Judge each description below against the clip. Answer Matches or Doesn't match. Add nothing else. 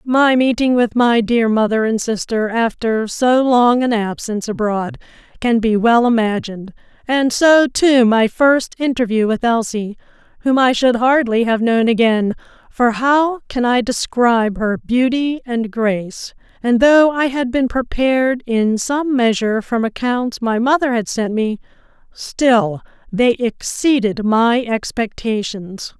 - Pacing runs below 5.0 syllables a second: Matches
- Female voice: Matches